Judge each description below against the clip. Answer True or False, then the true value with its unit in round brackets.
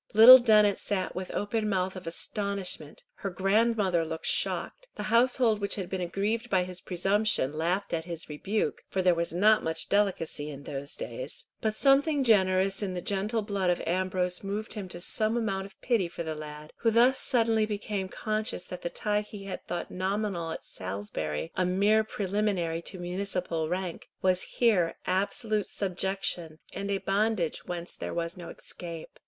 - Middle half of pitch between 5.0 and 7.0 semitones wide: False (3.4 semitones)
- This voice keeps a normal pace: True (175 wpm)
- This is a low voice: False (195 Hz)